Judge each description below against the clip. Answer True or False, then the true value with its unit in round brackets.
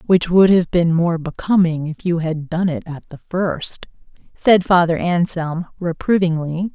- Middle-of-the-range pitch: True (170 Hz)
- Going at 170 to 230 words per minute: False (160 wpm)